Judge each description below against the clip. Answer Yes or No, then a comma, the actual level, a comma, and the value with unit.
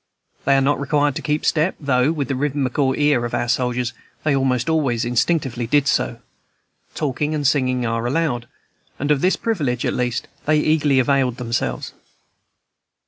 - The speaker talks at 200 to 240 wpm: No, average, 165 wpm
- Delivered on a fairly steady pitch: No, average, 3.2 semitones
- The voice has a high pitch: No, low, 135 Hz